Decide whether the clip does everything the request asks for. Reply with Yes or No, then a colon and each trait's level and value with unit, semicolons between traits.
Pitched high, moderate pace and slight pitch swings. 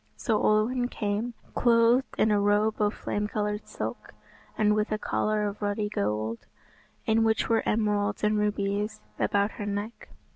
Yes: high, 210 Hz; average, 155 wpm; narrow, 1.3 semitones